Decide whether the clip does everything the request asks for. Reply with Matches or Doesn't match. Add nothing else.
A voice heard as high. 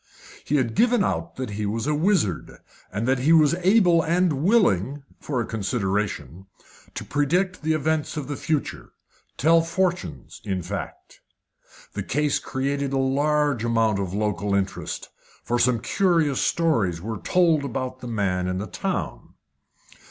Doesn't match